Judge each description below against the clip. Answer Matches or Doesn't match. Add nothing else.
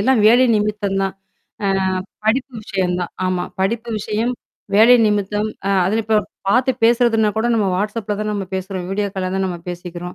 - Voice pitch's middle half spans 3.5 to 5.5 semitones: Doesn't match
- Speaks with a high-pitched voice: Matches